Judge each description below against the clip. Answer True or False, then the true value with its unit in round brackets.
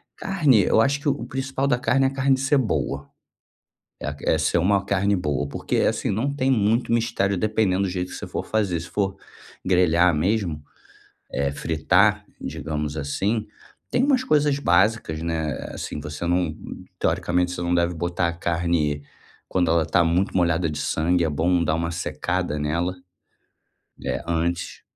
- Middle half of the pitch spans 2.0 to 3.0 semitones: False (5.0 semitones)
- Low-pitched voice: True (90 Hz)